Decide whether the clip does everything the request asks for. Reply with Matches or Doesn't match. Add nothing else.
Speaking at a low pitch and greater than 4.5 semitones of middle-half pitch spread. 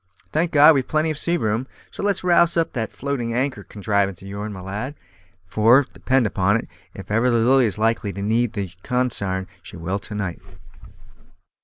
Matches